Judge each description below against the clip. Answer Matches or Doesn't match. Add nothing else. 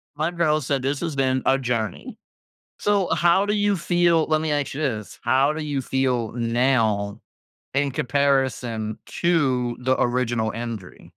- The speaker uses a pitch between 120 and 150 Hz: Matches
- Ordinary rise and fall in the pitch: Matches